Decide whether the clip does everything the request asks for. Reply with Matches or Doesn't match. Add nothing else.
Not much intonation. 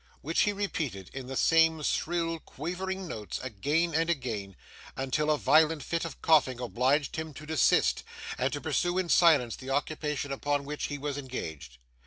Doesn't match